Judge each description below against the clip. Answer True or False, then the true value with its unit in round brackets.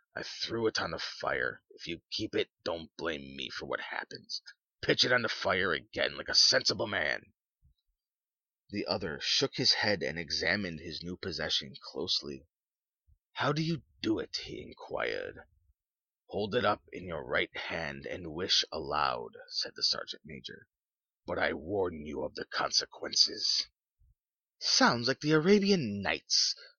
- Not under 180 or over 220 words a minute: False (155 wpm)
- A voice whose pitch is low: True (130 Hz)